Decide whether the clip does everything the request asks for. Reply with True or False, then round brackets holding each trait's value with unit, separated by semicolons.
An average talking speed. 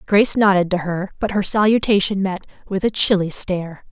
True (185 wpm)